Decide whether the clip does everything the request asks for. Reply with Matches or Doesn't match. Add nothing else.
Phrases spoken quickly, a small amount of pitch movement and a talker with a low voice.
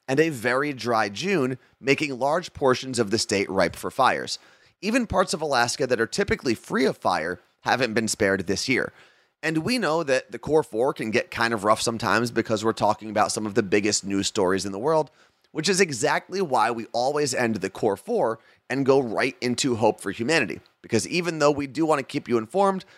Doesn't match